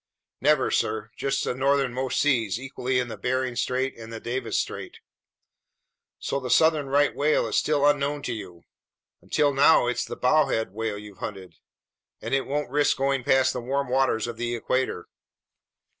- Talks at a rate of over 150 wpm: Yes, average, 170 wpm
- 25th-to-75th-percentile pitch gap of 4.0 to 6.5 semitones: No, average, 3.1 semitones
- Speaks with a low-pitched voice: Yes, low, 130 Hz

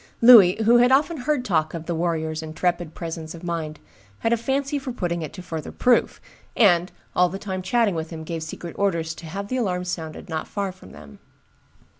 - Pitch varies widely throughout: Yes, wide, 5.7 semitones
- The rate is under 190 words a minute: No, fast, 205 wpm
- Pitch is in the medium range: Yes, medium, 175 Hz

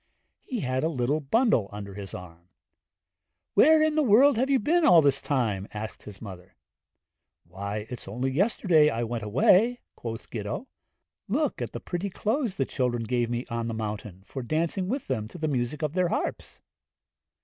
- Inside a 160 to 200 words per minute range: Yes, average, 180 wpm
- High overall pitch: No, low, 130 Hz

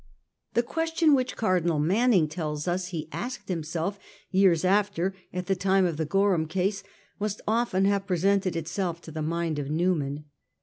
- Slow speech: No, average, 165 wpm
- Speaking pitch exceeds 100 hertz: Yes, medium, 185 Hz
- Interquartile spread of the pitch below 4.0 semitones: Yes, average, 3.6 semitones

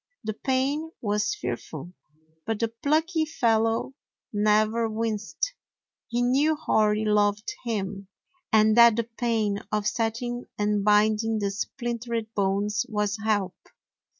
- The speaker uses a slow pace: Yes, slow, 120 wpm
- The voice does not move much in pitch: Yes, narrow, 2.2 semitones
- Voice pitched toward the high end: Yes, high, 220 Hz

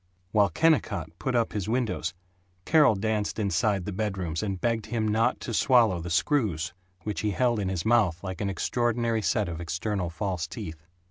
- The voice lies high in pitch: No, low, 105 Hz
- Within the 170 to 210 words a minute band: Yes, average, 180 wpm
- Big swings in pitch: No, average, 4.5 semitones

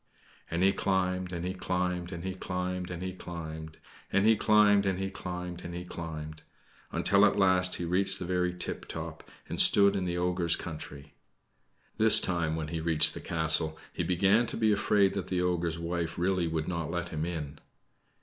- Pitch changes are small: Yes, narrow, 2.1 semitones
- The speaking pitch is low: Yes, very low, 90 Hz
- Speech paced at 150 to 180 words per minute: No, average, 190 wpm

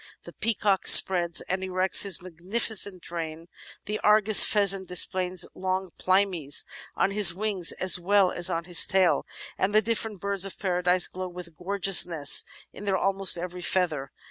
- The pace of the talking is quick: No, average, 155 wpm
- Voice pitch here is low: No, medium, 185 Hz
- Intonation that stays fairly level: Yes, narrow, 2.0 semitones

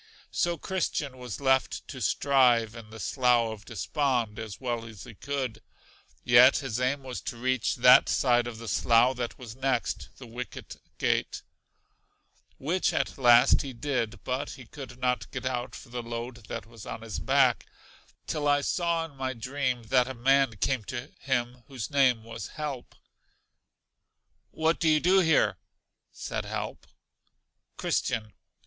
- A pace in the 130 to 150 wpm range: No, average, 160 wpm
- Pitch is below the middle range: Yes, low, 125 Hz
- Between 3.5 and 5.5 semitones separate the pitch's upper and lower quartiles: No, average, 2.7 semitones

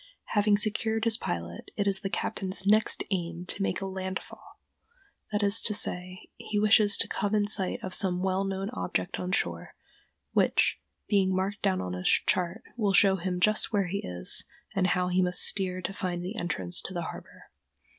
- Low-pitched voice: No, high, 190 Hz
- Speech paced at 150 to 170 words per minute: No, average, 190 wpm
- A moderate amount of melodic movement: No, narrow, 2.3 semitones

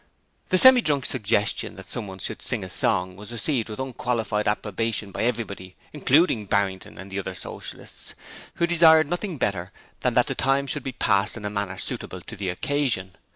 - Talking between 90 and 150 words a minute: No, average, 185 wpm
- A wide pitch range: Yes, wide, 5.7 semitones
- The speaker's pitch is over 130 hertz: No, low, 110 Hz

